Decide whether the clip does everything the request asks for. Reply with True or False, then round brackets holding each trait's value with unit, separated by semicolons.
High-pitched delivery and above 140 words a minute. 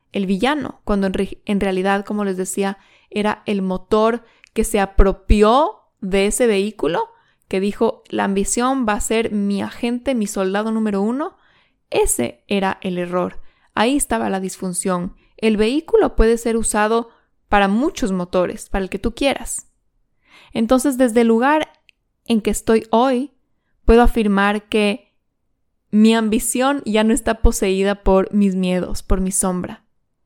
True (215 Hz; 150 wpm)